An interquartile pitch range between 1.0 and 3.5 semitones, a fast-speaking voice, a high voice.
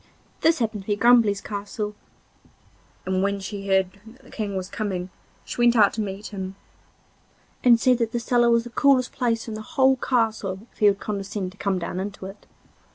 Yes: average, 3.2 semitones; fast, 210 wpm; high, 210 Hz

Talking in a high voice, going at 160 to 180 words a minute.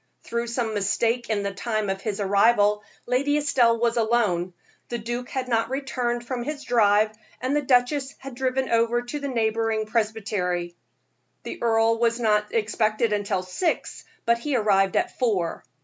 Yes: high, 230 Hz; average, 165 wpm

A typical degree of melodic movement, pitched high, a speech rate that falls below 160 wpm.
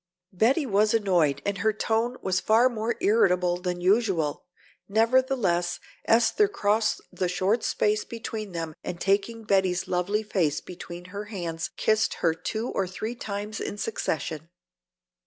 Yes: average, 3.7 semitones; high, 200 Hz; average, 140 wpm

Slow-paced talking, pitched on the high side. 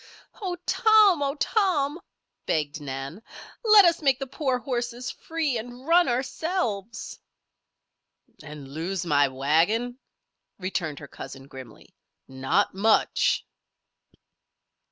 Yes: slow, 105 wpm; high, 240 Hz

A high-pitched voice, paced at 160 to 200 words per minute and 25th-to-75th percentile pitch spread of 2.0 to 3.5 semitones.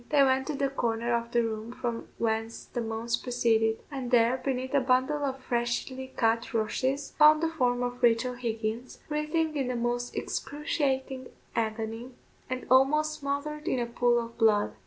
Yes: high, 245 Hz; average, 170 wpm; average, 2.8 semitones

